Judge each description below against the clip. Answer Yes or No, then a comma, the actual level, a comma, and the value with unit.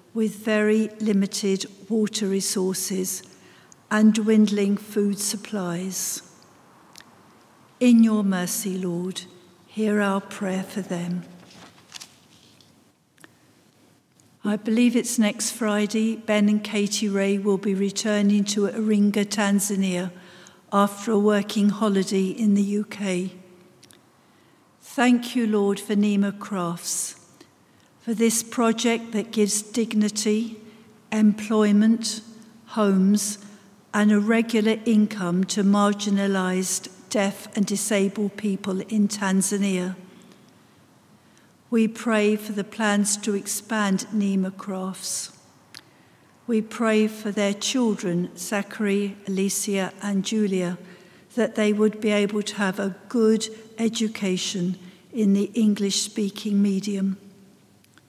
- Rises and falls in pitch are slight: Yes, narrow, 1.9 semitones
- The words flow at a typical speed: No, slow, 100 wpm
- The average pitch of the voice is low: No, high, 205 Hz